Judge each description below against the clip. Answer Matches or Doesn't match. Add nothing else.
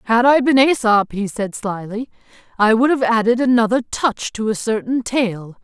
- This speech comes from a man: Doesn't match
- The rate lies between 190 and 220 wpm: Doesn't match